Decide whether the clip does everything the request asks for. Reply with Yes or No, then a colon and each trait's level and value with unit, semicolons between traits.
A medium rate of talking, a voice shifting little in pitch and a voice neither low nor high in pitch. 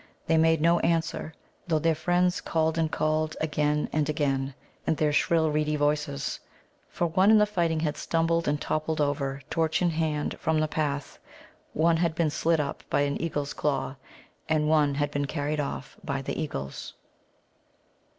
Yes: average, 170 wpm; narrow, 1.9 semitones; medium, 155 Hz